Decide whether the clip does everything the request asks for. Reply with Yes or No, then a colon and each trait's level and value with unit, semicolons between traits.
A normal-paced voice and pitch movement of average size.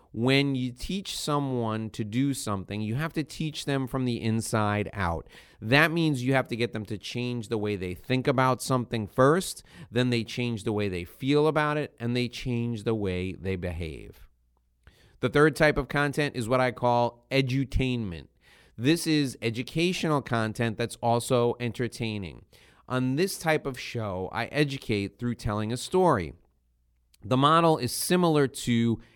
Yes: average, 165 wpm; average, 4.4 semitones